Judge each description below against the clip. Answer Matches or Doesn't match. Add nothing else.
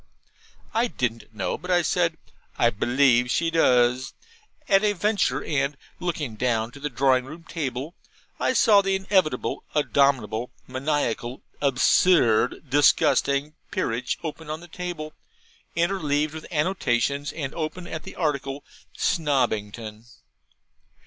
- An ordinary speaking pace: Doesn't match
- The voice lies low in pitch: Doesn't match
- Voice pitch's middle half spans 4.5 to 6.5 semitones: Matches